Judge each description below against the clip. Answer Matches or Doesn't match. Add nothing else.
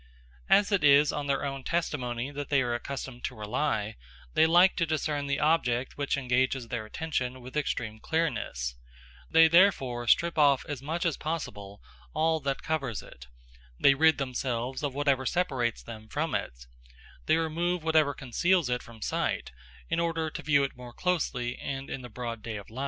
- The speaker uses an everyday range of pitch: Matches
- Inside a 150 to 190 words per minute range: Matches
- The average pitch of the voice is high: Doesn't match